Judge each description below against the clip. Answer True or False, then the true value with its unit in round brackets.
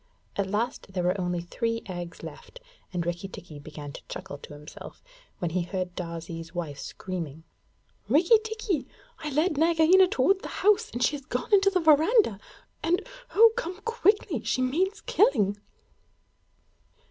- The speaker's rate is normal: True (155 wpm)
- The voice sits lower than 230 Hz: False (245 Hz)